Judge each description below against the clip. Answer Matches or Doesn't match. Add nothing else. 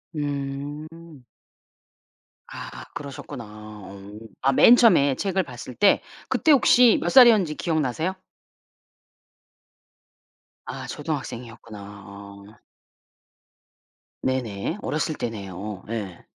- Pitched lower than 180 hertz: Matches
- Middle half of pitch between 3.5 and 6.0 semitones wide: Doesn't match